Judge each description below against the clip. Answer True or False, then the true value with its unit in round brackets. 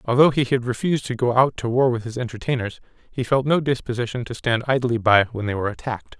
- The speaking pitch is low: True (120 Hz)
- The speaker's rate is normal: False (230 wpm)